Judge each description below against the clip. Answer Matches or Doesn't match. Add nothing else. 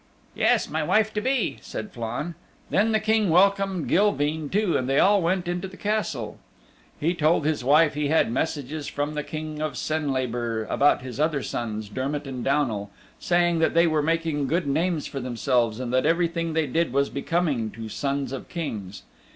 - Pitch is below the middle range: Doesn't match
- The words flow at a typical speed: Matches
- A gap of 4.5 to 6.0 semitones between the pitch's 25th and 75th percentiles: Matches